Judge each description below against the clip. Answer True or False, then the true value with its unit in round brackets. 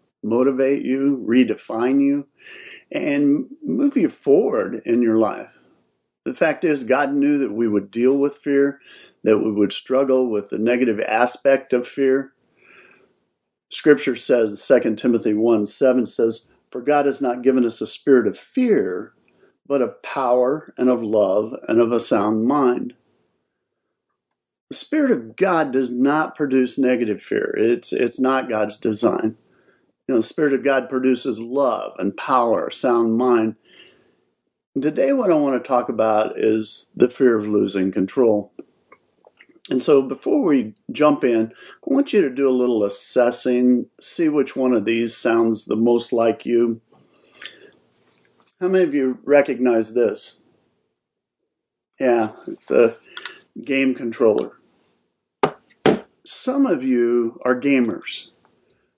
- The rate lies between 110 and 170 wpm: True (140 wpm)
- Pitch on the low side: True (130 Hz)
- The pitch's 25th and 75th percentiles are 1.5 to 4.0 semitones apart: False (4.4 semitones)